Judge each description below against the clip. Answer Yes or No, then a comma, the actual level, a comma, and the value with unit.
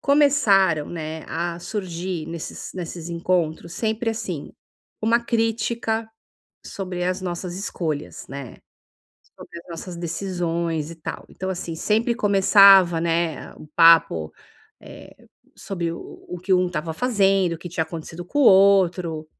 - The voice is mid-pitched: Yes, medium, 175 Hz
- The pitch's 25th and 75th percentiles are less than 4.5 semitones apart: Yes, average, 3.1 semitones